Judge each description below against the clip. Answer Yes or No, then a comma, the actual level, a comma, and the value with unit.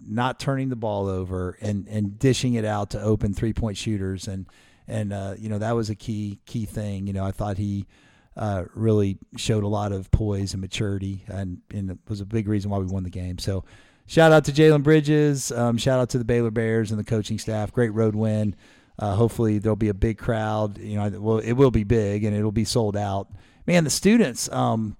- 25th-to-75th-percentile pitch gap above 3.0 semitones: No, narrow, 2.6 semitones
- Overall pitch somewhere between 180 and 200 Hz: No, low, 110 Hz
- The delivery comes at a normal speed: No, fast, 230 wpm